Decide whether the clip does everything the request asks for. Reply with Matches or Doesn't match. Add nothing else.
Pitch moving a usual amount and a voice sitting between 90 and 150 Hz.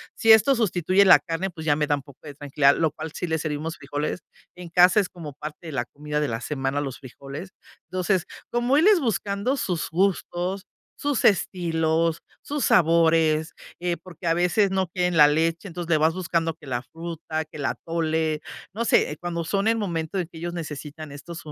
Doesn't match